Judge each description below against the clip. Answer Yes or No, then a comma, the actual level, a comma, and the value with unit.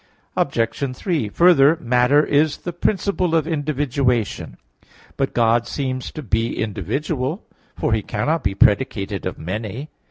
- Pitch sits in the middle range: No, low, 130 Hz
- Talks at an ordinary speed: No, slow, 130 wpm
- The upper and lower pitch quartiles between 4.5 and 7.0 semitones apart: Yes, wide, 5.5 semitones